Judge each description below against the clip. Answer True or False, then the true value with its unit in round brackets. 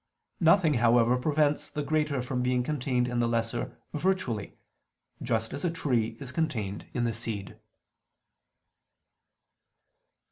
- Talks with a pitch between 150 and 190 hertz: False (125 Hz)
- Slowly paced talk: True (120 wpm)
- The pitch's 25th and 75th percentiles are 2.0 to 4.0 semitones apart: False (4.5 semitones)